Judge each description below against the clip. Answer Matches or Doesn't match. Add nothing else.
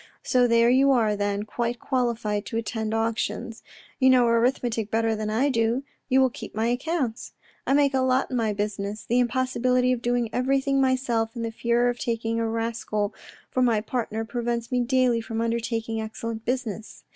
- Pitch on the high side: Matches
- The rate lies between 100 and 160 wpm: Doesn't match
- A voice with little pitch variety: Matches